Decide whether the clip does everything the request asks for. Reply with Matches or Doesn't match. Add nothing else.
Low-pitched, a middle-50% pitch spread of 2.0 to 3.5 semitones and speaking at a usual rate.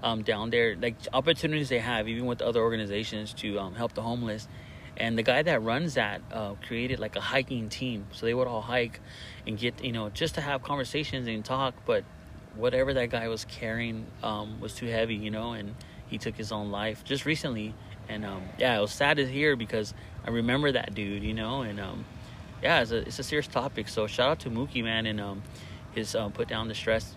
Doesn't match